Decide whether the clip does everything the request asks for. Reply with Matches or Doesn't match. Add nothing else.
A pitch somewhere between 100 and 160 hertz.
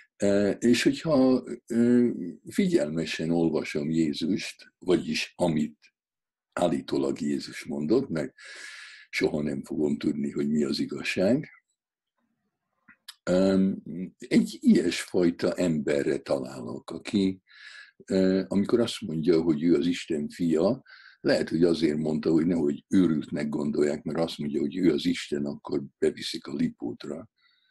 Doesn't match